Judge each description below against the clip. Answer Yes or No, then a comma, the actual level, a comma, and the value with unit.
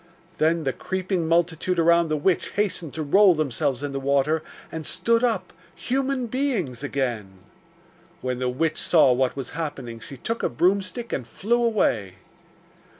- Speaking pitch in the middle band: Yes, medium, 160 Hz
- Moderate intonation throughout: No, wide, 6.3 semitones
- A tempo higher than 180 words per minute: No, average, 155 wpm